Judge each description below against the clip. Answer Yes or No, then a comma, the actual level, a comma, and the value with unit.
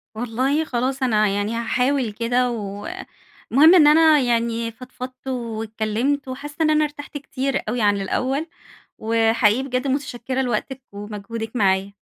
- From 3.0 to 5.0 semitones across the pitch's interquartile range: Yes, average, 3.5 semitones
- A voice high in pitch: Yes, high, 245 Hz